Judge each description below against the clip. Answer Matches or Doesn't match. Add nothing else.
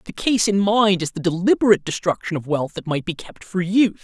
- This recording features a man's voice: Matches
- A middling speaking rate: Doesn't match